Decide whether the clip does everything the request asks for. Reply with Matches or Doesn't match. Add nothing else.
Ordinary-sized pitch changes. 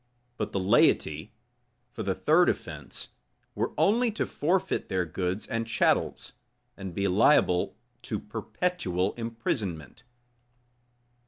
Doesn't match